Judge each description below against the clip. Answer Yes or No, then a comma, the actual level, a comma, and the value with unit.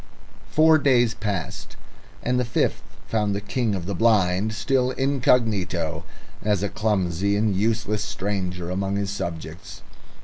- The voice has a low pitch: Yes, low, 105 Hz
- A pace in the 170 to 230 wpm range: No, slow, 135 wpm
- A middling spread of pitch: Yes, average, 3.4 semitones